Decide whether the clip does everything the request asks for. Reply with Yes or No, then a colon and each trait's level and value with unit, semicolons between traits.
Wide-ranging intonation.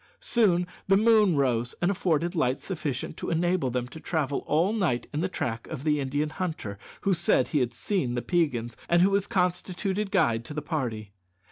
Yes: wide, 6.4 semitones